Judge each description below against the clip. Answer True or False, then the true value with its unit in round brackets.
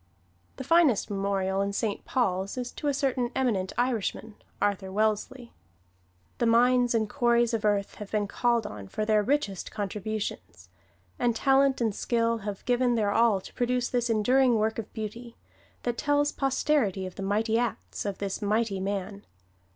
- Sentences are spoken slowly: False (165 wpm)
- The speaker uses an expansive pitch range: False (3.3 semitones)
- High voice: True (220 Hz)